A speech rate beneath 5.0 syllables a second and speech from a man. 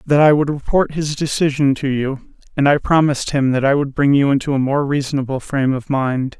No: 5.6 syllables/s; male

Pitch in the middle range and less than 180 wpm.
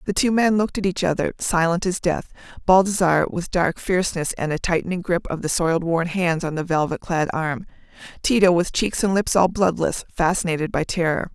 No: medium, 175 Hz; average, 200 wpm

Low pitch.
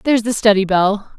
No: high, 210 Hz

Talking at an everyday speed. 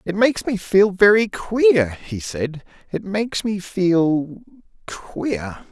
No: slow, 125 wpm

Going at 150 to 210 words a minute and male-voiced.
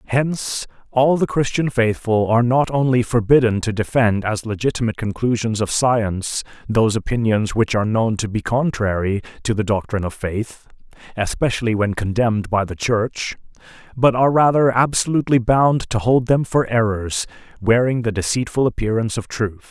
Yes: average, 155 wpm; male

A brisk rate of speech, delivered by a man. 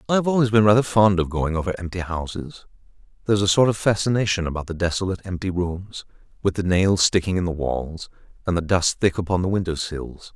Yes: fast, 210 wpm; male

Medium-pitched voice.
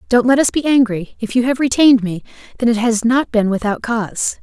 No: high, 235 Hz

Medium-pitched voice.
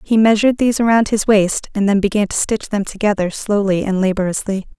No: high, 205 Hz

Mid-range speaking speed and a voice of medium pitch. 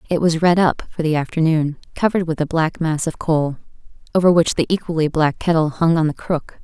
No: fast, 215 wpm; medium, 160 Hz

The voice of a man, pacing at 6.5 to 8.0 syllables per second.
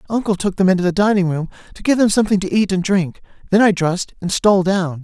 Yes: male; 6.6 syllables/s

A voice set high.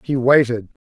No: low, 125 Hz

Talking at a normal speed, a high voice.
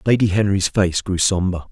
No: average, 175 wpm; very low, 95 Hz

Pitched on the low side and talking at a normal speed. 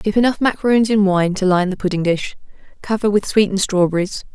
No: high, 200 Hz; average, 195 wpm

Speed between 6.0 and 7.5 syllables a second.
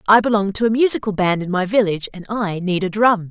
Yes: 6.2 syllables/s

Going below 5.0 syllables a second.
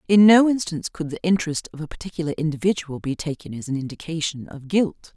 No: 6.4 syllables/s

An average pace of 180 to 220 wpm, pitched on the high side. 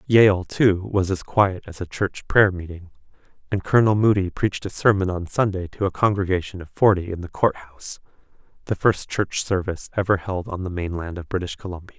No: average, 190 wpm; very low, 95 Hz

